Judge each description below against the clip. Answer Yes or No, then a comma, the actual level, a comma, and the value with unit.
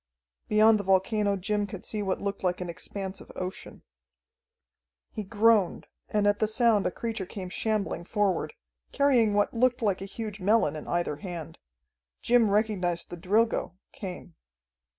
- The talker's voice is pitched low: No, high, 205 Hz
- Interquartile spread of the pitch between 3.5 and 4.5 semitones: No, average, 2.9 semitones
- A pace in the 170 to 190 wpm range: No, average, 155 wpm